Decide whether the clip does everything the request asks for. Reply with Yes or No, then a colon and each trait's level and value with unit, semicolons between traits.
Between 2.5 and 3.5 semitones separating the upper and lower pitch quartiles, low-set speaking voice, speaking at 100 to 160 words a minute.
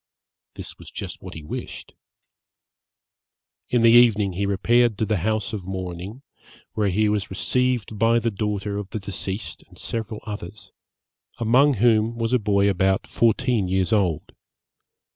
Yes: average, 3.1 semitones; low, 105 Hz; average, 150 wpm